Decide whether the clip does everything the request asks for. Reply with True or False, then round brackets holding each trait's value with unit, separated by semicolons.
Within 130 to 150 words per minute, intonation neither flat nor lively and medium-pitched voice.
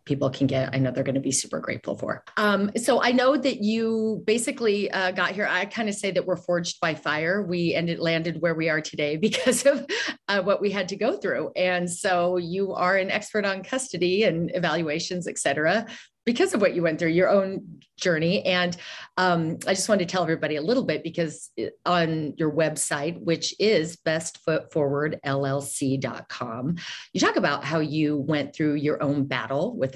False (195 wpm; 4.5 semitones; 175 Hz)